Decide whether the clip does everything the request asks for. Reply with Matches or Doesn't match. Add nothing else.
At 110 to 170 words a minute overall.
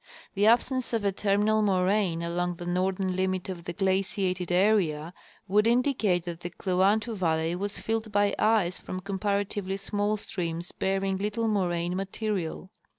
Matches